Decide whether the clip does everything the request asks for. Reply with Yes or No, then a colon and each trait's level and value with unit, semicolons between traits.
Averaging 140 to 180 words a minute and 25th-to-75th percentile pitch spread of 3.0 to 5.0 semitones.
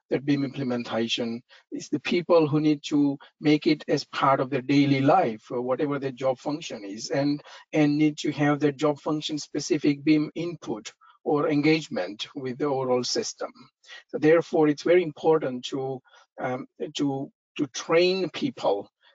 No: average, 160 wpm; narrow, 2.6 semitones